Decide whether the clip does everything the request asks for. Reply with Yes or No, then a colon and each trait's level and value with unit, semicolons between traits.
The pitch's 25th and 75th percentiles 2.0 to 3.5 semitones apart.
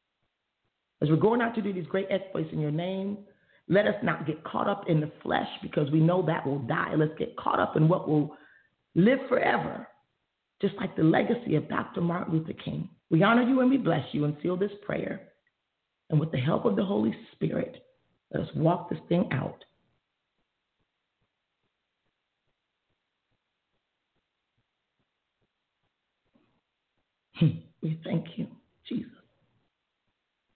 No: average, 4.2 semitones